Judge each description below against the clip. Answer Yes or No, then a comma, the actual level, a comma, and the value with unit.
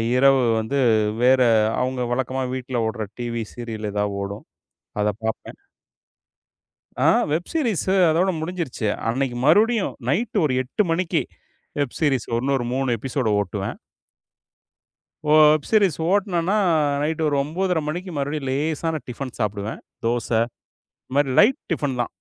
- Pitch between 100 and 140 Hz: Yes, low, 135 Hz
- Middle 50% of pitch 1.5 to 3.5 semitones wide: No, average, 5.3 semitones